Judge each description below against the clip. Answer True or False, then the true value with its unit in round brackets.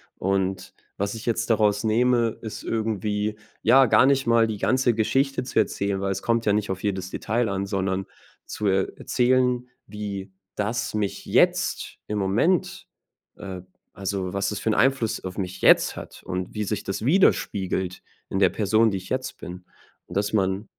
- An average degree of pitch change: True (3.1 semitones)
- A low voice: True (105 Hz)